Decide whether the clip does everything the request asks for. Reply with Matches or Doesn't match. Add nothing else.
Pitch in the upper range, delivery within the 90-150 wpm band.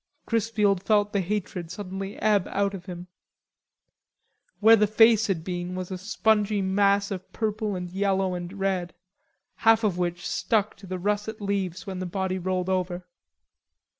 Doesn't match